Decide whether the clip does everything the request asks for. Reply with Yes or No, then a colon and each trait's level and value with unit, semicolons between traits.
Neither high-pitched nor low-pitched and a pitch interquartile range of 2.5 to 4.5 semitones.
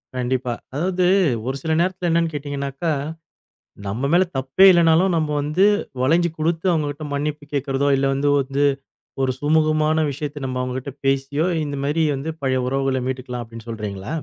Yes: medium, 145 Hz; average, 3.3 semitones